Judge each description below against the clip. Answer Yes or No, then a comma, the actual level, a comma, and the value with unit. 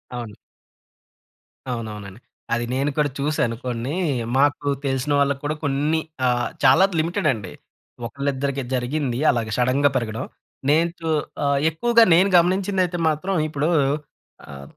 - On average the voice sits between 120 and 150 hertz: Yes, medium, 140 Hz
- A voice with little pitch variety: No, average, 4.2 semitones